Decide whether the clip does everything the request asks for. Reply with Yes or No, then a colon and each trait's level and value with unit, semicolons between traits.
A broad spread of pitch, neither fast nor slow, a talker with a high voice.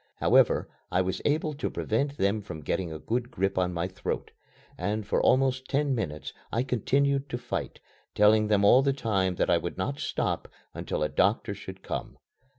No: wide, 6.0 semitones; average, 185 wpm; low, 110 Hz